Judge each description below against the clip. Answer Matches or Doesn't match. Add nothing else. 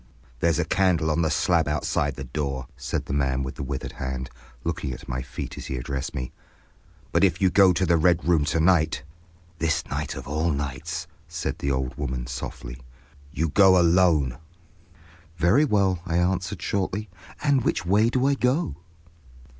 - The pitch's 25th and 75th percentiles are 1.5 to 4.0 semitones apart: Doesn't match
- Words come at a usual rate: Matches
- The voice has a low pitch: Matches